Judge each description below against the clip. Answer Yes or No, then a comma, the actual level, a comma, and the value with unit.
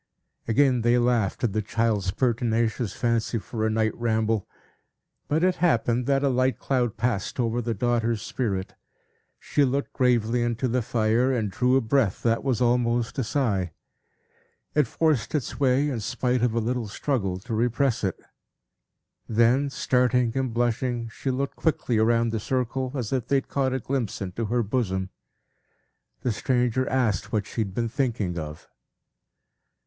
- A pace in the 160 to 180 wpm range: Yes, average, 165 wpm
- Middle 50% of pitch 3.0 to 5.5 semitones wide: No, narrow, 2.6 semitones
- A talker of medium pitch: No, low, 120 Hz